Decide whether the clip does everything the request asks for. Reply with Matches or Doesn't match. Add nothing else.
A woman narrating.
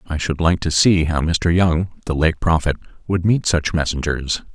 Doesn't match